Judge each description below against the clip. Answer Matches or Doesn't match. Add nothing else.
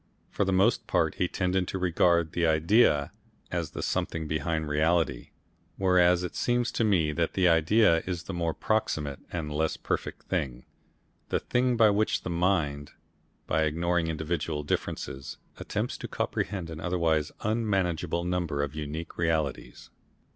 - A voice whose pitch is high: Doesn't match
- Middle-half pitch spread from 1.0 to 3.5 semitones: Matches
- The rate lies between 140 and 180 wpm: Matches